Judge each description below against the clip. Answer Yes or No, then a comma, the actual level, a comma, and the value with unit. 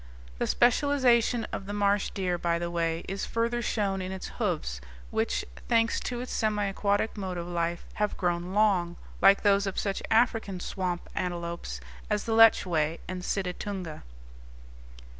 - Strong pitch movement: No, average, 3.8 semitones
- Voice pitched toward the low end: No, high, 195 Hz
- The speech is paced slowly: No, average, 155 wpm